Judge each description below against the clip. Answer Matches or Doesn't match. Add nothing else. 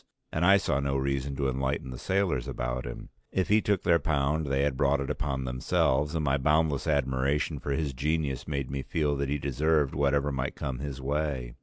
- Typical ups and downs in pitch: Doesn't match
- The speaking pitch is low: Matches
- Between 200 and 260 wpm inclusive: Matches